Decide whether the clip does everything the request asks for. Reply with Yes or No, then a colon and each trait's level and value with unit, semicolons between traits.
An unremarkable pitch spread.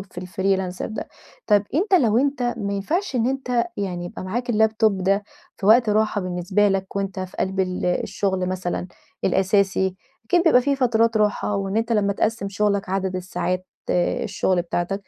Yes: average, 3.3 semitones